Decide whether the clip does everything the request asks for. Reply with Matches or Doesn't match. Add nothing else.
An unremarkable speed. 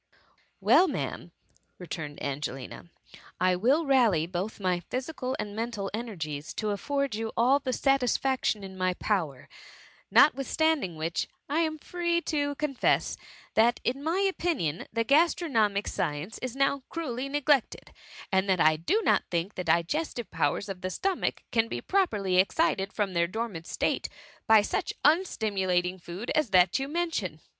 Matches